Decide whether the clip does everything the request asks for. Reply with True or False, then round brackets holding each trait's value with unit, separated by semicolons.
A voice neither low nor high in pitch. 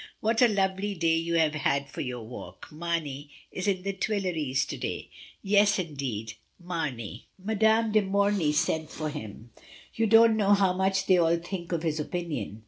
True (170 Hz)